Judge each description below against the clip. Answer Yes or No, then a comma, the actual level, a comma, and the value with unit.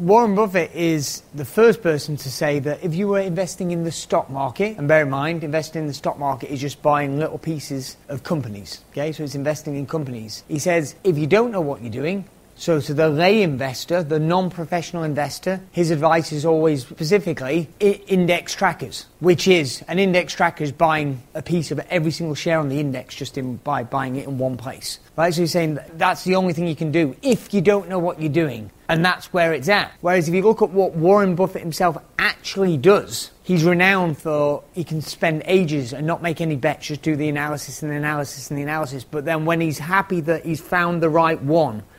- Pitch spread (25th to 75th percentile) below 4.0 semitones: Yes, average, 3.3 semitones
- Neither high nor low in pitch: Yes, medium, 160 Hz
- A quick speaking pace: Yes, fast, 225 wpm